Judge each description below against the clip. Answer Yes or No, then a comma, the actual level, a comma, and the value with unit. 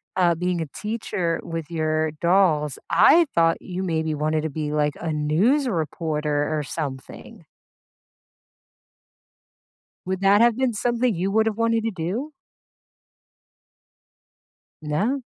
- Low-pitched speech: No, medium, 170 Hz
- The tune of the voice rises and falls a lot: Yes, wide, 5.7 semitones